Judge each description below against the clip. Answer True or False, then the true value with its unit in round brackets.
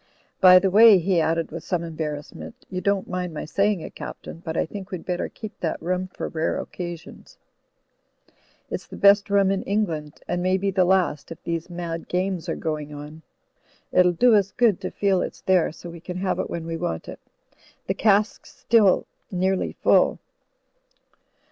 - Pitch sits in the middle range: True (180 Hz)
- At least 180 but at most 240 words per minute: True (185 wpm)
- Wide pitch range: False (2.9 semitones)